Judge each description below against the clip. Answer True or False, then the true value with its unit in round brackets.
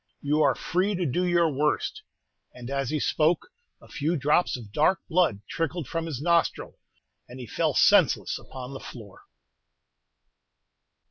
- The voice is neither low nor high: True (150 Hz)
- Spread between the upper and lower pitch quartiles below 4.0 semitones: False (4.6 semitones)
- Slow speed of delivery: False (150 wpm)